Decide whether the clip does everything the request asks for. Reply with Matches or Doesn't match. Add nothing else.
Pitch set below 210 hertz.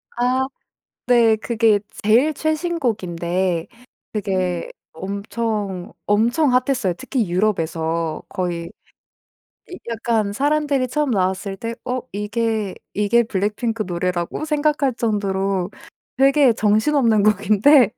Doesn't match